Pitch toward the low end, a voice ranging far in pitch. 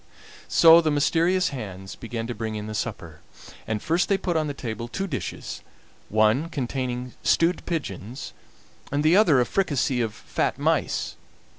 Yes: low, 130 Hz; wide, 6.7 semitones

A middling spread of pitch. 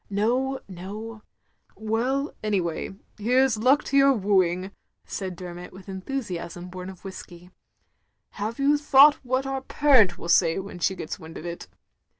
No: wide, 6.5 semitones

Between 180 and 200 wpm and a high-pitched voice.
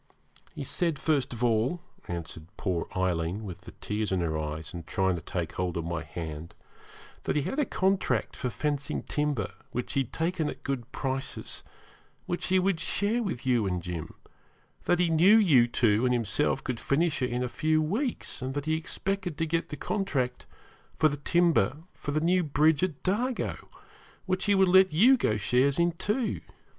No: average, 190 wpm; medium, 140 Hz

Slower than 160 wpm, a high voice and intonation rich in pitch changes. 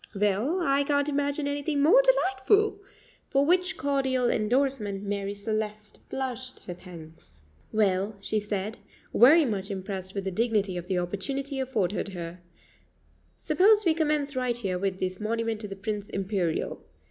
Yes: average, 145 wpm; high, 220 Hz; wide, 6.4 semitones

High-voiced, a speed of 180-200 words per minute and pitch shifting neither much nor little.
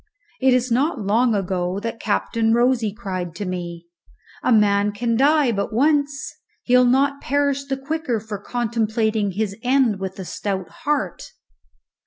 No: high, 230 Hz; average, 150 wpm; average, 4.7 semitones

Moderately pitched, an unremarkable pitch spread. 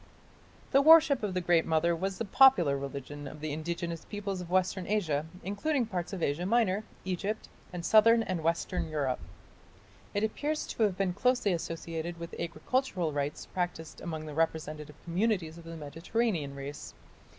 Yes: medium, 175 Hz; average, 4.5 semitones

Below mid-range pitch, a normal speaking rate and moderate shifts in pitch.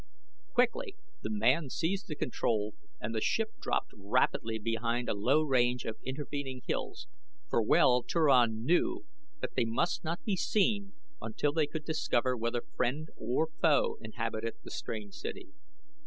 No: low, 130 Hz; average, 150 wpm; wide, 6.6 semitones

